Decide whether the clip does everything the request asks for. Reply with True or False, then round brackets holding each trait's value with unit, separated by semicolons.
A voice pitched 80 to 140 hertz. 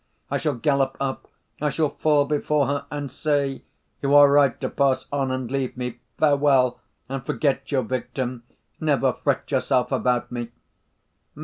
True (135 Hz)